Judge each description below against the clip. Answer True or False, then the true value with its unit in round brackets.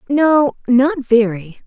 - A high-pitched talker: True (260 Hz)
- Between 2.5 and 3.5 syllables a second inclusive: True (3.0 syllables/s)